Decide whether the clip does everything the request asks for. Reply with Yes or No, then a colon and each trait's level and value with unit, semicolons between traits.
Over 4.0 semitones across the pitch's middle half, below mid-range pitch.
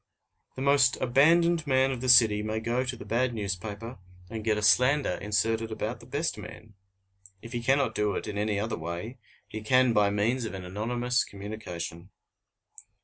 No: average, 3.5 semitones; low, 115 Hz